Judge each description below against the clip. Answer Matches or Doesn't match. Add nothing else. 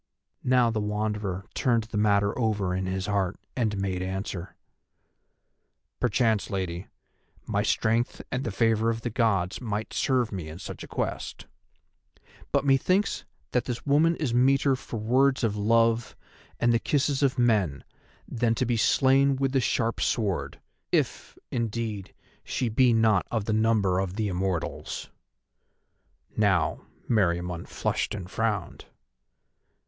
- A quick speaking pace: Doesn't match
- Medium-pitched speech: Doesn't match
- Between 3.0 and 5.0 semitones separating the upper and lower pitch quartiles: Matches